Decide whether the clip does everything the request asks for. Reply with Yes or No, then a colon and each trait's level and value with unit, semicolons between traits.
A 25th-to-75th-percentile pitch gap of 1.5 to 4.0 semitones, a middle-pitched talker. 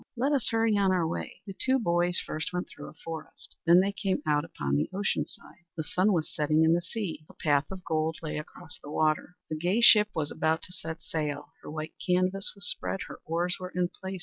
Yes: average, 3.5 semitones; medium, 175 Hz